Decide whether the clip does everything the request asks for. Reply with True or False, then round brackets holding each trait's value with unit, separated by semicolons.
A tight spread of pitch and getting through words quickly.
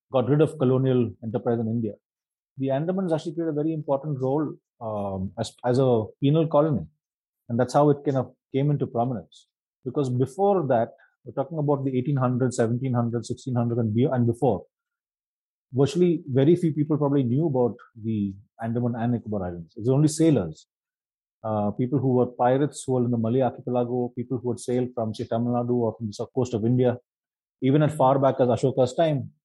False (3.2 semitones; 185 wpm)